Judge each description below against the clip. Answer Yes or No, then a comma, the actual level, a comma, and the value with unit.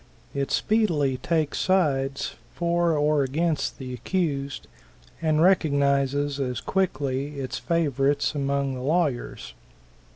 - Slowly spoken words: Yes, slow, 105 wpm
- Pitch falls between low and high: Yes, medium, 145 Hz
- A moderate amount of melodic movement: Yes, average, 3.3 semitones